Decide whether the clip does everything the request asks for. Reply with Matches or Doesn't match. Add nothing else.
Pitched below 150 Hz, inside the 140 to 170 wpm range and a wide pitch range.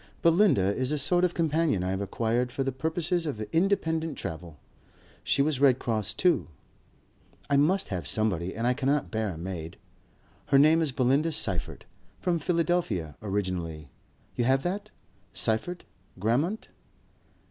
Matches